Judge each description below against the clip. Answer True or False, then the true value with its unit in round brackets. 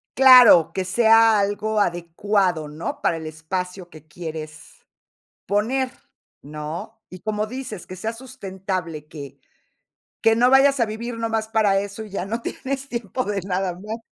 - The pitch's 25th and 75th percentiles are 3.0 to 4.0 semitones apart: False (4.5 semitones)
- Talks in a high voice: True (205 Hz)